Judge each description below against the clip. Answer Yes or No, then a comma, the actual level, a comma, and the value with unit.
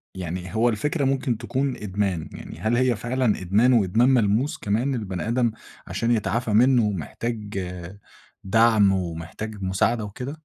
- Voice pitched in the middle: No, low, 110 Hz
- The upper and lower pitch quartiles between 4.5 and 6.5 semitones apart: No, average, 3.9 semitones